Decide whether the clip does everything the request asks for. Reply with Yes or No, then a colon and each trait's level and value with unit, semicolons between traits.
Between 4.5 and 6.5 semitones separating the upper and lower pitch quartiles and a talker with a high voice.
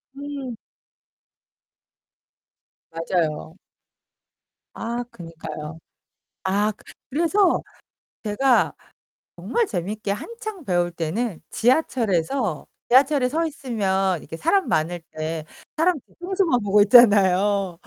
No: wide, 7.9 semitones; high, 210 Hz